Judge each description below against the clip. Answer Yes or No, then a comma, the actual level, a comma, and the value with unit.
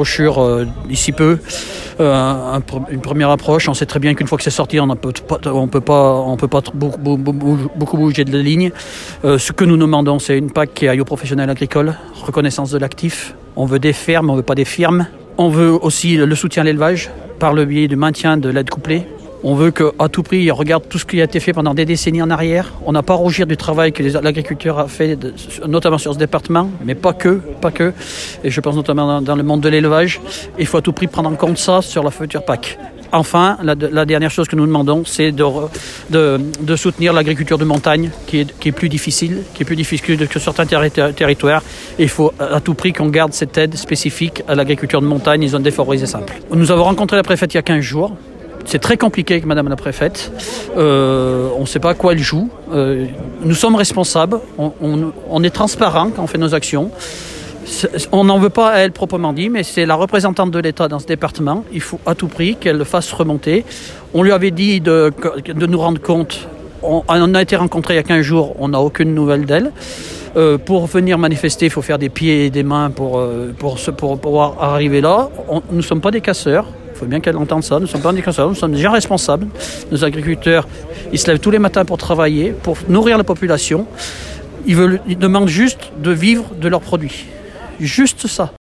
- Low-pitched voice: No, medium, 155 Hz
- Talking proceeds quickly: Yes, fast, 230 wpm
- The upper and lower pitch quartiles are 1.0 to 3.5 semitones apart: Yes, average, 2.8 semitones